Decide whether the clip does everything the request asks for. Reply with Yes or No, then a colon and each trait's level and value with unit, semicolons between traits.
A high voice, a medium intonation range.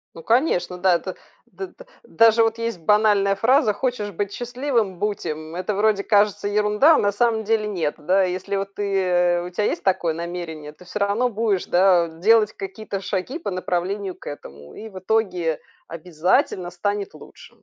Yes: high, 200 Hz; average, 3.5 semitones